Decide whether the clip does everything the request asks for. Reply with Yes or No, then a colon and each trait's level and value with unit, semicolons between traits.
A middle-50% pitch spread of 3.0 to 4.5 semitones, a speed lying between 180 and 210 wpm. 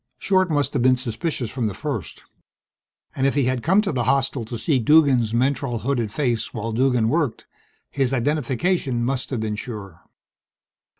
No: average, 3.4 semitones; average, 170 wpm